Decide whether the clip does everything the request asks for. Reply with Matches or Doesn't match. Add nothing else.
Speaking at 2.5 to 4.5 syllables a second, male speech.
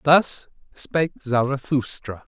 Matches